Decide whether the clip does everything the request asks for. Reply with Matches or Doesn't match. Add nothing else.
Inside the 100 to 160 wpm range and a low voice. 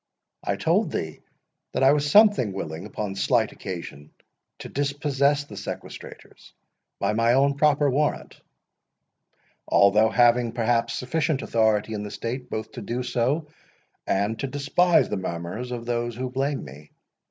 Matches